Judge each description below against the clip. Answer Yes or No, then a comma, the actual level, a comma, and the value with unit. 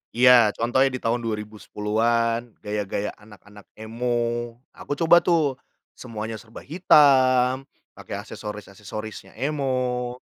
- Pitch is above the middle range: No, low, 120 Hz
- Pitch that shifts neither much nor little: Yes, average, 3.4 semitones